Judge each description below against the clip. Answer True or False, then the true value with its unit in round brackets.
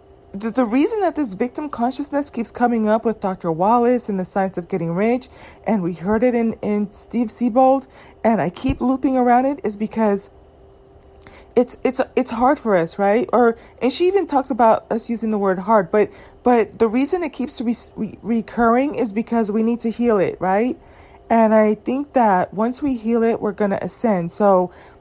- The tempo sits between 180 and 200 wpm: True (195 wpm)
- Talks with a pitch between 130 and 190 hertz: False (230 Hz)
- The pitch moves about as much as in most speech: True (3.1 semitones)